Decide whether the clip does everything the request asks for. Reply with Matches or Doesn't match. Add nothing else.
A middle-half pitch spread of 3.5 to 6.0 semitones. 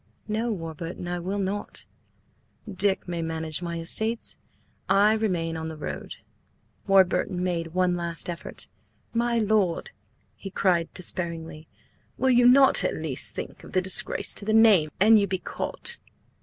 Matches